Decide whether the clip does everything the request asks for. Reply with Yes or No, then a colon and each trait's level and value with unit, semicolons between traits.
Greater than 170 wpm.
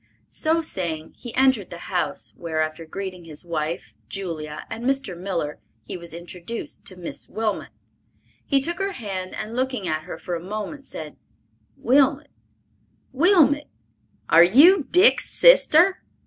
No: average, 145 wpm